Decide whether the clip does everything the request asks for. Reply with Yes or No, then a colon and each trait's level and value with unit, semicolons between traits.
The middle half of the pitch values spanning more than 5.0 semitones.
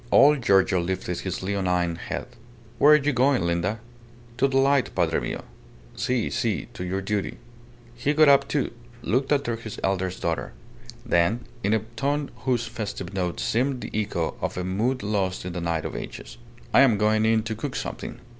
Yes: wide, 5.6 semitones